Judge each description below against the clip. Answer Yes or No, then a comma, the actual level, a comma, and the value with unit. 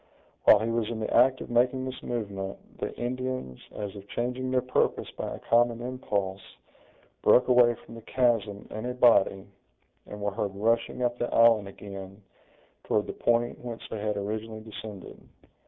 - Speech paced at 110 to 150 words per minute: No, average, 170 wpm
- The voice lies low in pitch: Yes, low, 115 Hz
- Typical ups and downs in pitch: Yes, average, 3.0 semitones